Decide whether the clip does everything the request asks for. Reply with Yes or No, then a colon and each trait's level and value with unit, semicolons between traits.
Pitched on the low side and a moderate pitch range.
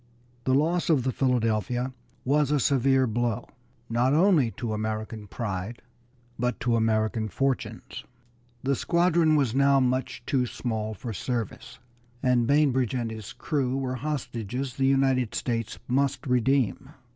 Yes: low, 125 Hz; average, 3.1 semitones